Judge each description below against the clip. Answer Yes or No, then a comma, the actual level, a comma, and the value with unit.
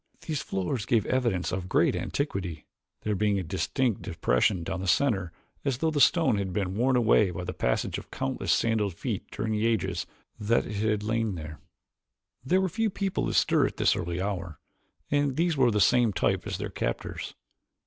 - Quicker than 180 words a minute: Yes, average, 190 wpm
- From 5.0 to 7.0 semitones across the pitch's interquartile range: Yes, wide, 5.6 semitones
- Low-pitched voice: Yes, low, 105 Hz